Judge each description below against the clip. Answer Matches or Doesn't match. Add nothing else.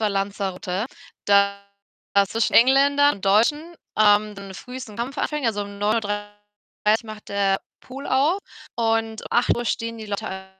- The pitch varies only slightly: Doesn't match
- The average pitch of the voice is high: Matches